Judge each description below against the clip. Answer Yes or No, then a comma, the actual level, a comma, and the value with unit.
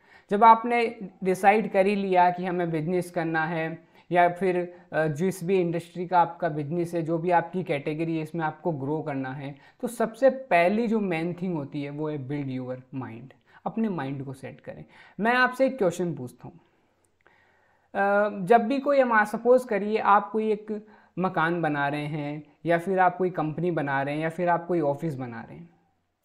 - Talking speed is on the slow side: No, average, 185 wpm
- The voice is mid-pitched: Yes, medium, 175 Hz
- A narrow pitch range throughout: No, average, 4.4 semitones